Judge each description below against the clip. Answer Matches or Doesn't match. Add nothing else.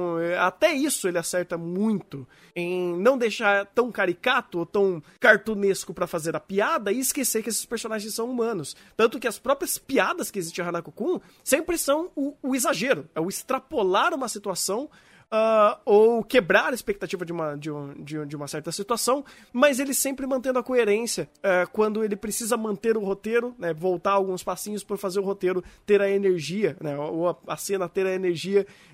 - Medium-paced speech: Doesn't match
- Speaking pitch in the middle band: Doesn't match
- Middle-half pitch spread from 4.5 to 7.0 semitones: Matches